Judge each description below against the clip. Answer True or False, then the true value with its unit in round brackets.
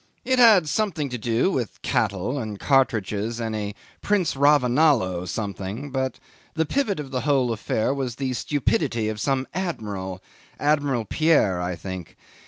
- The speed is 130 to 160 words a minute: True (150 wpm)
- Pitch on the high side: False (125 Hz)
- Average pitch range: False (5.7 semitones)